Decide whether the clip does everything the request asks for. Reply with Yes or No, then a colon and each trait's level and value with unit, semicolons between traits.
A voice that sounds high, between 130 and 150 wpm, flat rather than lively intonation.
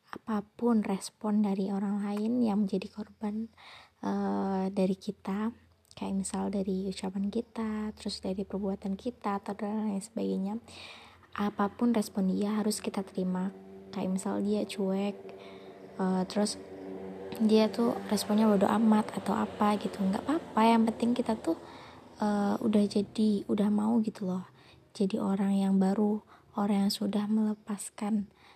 Yes: high, 205 Hz; average, 135 wpm; narrow, 1.8 semitones